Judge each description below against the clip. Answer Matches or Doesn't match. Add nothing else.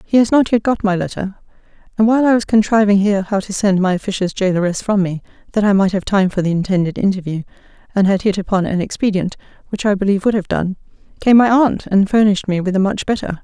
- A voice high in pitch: Matches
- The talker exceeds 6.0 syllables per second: Matches